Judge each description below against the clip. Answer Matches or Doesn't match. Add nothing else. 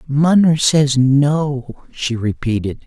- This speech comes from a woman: Doesn't match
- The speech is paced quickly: Doesn't match